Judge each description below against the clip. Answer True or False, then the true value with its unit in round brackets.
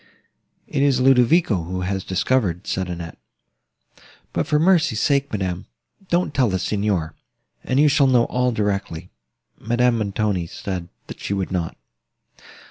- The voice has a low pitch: True (105 Hz)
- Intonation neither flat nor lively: False (6.0 semitones)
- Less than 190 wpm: True (140 wpm)